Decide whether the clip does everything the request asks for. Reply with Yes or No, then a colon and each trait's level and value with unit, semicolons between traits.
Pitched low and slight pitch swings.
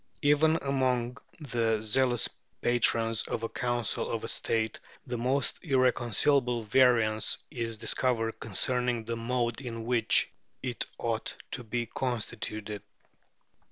Yes: low, 120 Hz; narrow, 2.0 semitones